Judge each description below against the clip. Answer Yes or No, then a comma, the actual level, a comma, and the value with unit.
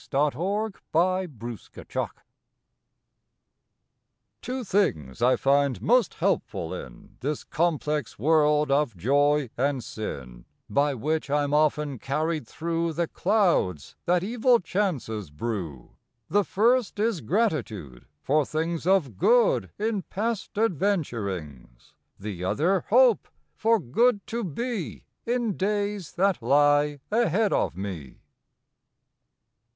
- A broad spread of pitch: Yes, wide, 8.3 semitones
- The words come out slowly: Yes, slow, 110 wpm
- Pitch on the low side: No, medium, 155 Hz